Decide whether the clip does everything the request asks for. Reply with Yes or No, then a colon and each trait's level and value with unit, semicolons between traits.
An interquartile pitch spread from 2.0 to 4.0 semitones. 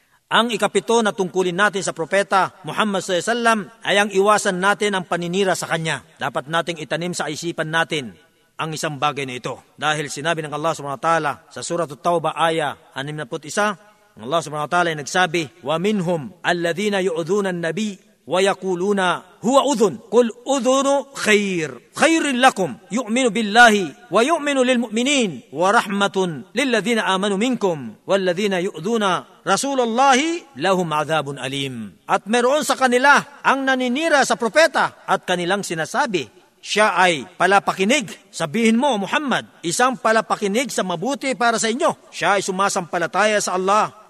No: wide, 5.4 semitones